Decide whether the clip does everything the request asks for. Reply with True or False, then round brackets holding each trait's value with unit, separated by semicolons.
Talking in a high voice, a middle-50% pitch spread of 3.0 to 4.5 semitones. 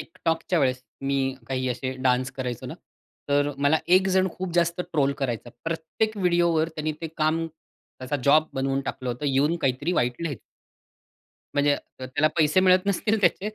False (150 Hz; 4.2 semitones)